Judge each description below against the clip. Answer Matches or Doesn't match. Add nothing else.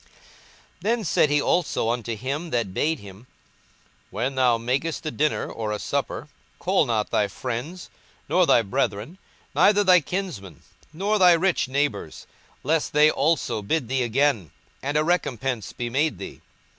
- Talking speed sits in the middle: Matches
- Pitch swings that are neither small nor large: Doesn't match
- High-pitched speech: Doesn't match